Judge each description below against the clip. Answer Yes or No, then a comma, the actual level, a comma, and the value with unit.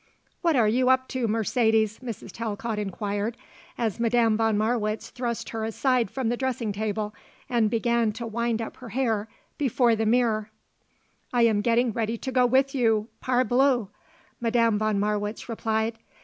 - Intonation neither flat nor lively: No, narrow, 2.1 semitones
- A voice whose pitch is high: Yes, high, 230 Hz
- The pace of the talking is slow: No, average, 160 wpm